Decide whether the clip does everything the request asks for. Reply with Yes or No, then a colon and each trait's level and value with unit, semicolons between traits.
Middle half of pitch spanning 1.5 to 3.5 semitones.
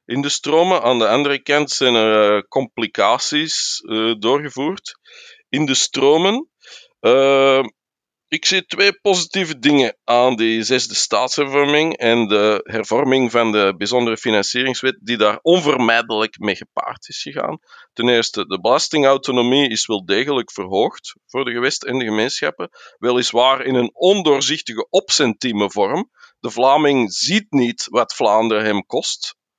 No: average, 4.5 semitones